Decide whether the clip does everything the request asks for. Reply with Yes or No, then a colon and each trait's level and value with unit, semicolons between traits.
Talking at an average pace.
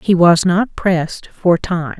Yes: average, 180 wpm